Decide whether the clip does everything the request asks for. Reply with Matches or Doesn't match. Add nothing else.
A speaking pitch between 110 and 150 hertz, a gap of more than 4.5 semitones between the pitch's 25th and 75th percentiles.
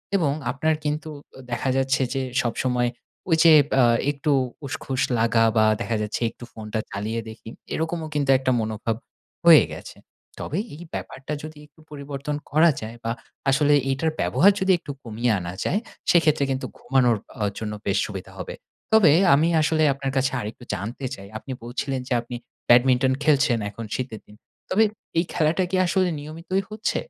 Matches